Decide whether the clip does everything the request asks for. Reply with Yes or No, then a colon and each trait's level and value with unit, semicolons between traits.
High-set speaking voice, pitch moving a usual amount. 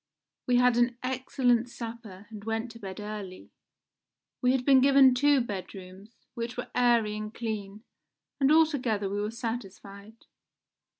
Yes: high, 230 Hz; average, 3.1 semitones